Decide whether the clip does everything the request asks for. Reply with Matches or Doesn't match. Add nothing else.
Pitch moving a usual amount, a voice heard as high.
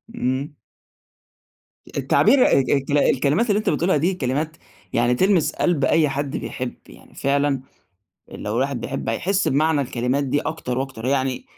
Doesn't match